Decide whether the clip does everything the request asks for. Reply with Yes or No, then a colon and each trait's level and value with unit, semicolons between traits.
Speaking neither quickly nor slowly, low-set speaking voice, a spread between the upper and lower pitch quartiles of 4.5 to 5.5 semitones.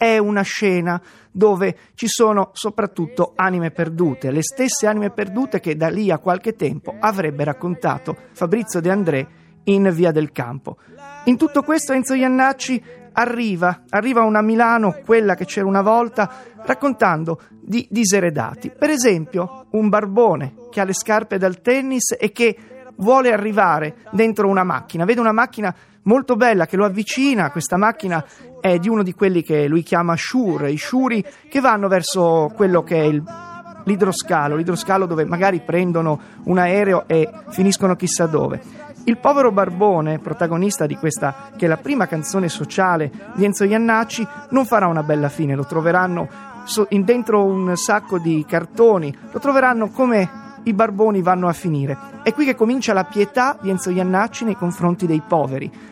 No: average, 160 wpm; high, 195 Hz; average, 5.0 semitones